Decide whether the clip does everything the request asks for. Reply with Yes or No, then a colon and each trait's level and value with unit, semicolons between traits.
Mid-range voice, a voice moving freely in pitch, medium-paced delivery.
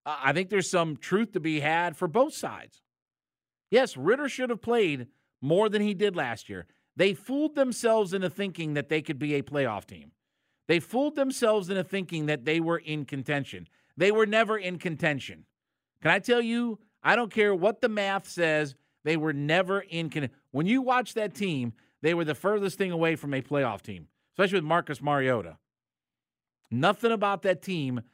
Yes: medium, 170 Hz; wide, 6.1 semitones; average, 190 wpm